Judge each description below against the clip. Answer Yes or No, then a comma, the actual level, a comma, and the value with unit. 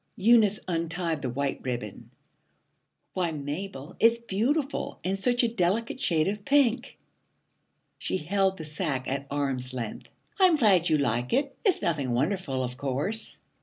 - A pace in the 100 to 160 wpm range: Yes, average, 145 wpm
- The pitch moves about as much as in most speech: No, wide, 7.9 semitones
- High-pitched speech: No, medium, 175 Hz